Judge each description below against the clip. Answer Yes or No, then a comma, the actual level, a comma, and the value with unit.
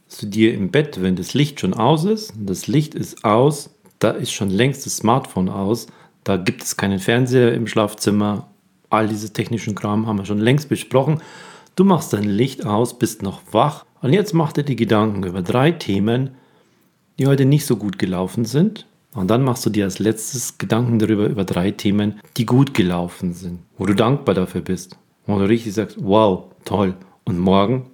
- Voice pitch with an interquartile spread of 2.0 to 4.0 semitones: No, average, 4.8 semitones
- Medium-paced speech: No, fast, 200 wpm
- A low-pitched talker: Yes, low, 110 Hz